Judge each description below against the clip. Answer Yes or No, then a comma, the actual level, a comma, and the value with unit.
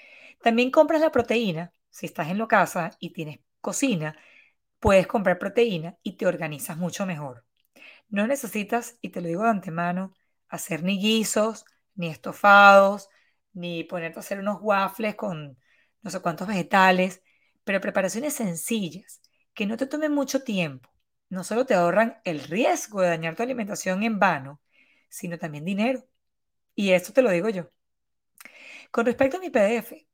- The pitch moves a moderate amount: Yes, average, 4.9 semitones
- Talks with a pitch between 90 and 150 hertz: No, high, 200 Hz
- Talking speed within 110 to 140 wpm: No, average, 155 wpm